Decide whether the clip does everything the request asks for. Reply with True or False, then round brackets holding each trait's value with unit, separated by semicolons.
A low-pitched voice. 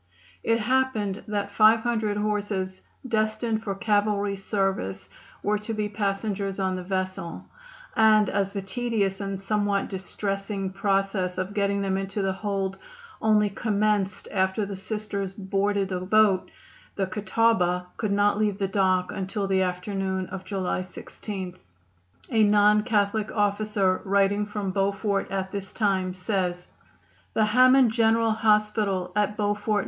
False (200 Hz)